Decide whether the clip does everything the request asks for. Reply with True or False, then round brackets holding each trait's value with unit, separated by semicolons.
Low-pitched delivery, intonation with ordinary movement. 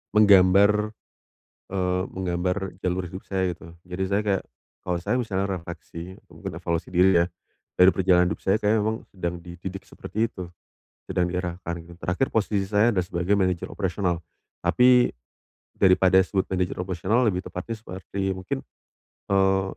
False (95 Hz; 1.8 semitones)